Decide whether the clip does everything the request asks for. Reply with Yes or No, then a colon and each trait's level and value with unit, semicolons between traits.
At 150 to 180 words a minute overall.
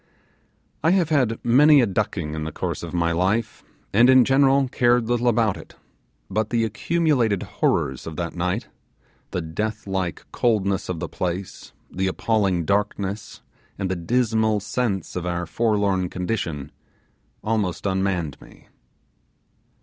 No: average, 140 wpm